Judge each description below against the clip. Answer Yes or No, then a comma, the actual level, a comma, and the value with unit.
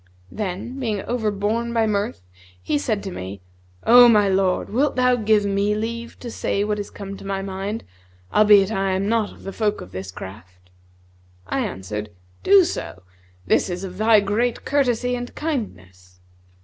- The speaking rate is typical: Yes, average, 170 wpm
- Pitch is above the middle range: Yes, high, 205 Hz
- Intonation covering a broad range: No, average, 3.6 semitones